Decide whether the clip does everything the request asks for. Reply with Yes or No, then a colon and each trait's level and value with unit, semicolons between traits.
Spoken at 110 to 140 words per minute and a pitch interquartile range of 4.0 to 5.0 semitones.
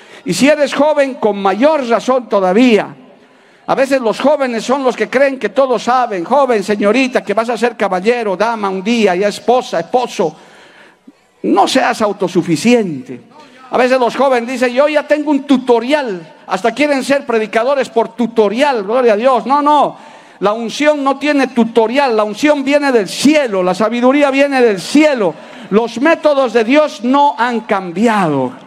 No: average, 165 wpm; average, 4.6 semitones